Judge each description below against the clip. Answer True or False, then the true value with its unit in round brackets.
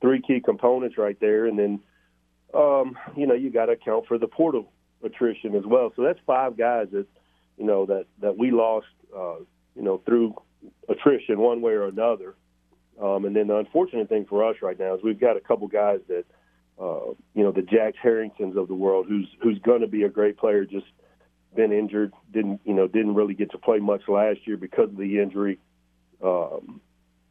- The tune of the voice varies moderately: True (3.7 semitones)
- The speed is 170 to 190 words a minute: False (205 wpm)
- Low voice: True (105 Hz)